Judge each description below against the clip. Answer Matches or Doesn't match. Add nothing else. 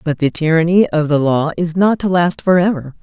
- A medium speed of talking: Doesn't match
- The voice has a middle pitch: Matches